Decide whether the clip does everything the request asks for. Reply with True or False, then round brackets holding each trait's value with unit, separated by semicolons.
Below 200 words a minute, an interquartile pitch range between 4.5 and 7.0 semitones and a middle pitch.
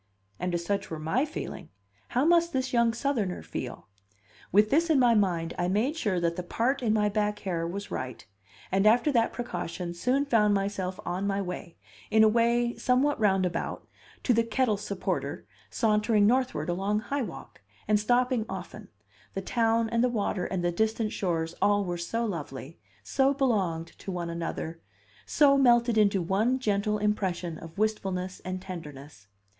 False (170 wpm; 4.8 semitones; 210 Hz)